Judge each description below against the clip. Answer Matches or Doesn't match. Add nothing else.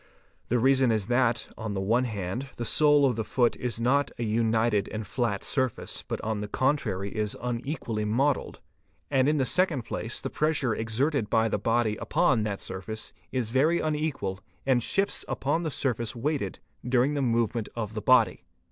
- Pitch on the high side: Doesn't match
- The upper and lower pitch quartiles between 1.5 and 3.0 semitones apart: Doesn't match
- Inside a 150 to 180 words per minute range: Doesn't match